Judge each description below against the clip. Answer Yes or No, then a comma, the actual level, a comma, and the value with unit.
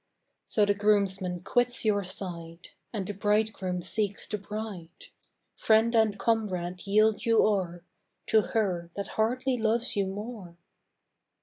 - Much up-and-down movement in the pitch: No, average, 3.0 semitones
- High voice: Yes, high, 205 Hz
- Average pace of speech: No, slow, 130 wpm